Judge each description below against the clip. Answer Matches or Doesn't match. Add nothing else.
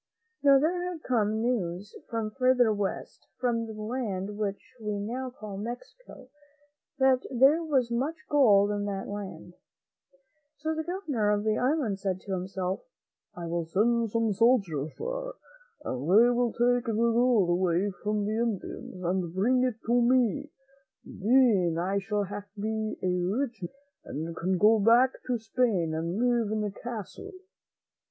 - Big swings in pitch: Doesn't match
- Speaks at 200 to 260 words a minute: Doesn't match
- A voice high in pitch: Matches